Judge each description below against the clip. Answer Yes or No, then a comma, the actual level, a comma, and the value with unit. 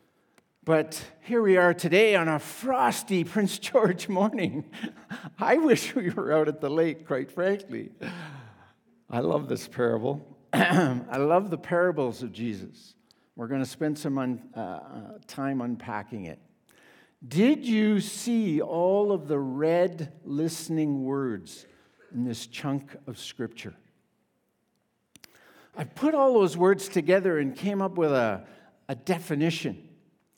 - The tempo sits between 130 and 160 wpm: Yes, slow, 135 wpm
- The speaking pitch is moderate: Yes, medium, 165 Hz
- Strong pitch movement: Yes, wide, 5.8 semitones